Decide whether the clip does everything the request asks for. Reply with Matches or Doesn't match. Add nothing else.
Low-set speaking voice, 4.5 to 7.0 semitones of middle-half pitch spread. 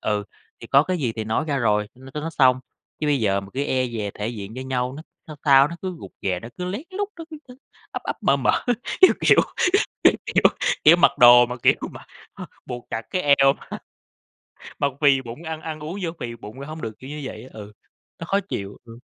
Matches